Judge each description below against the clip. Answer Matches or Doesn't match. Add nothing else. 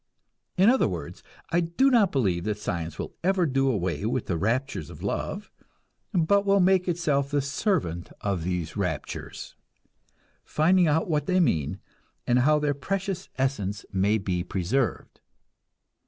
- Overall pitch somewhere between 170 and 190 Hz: Doesn't match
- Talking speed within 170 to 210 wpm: Doesn't match